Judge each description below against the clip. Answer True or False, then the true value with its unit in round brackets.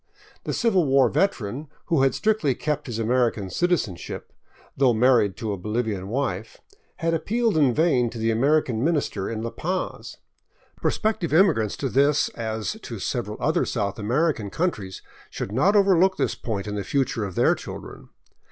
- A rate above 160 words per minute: True (170 wpm)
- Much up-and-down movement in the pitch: True (6.8 semitones)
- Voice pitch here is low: True (125 Hz)